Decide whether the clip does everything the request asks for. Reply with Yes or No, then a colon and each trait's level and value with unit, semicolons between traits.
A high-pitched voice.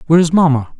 No: medium, 160 Hz